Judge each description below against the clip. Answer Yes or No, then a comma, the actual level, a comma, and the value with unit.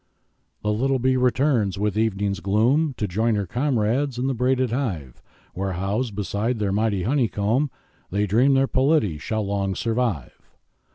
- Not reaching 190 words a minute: Yes, average, 155 wpm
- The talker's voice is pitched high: No, low, 110 Hz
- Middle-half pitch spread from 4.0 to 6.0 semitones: Yes, average, 4.4 semitones